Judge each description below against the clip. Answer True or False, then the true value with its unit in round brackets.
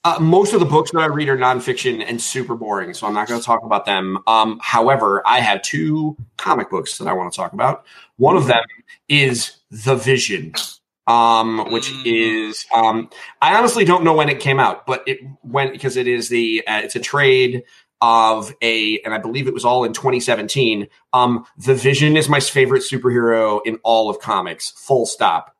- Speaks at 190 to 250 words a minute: True (200 wpm)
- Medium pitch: False (125 Hz)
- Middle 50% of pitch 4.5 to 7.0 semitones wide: False (3.5 semitones)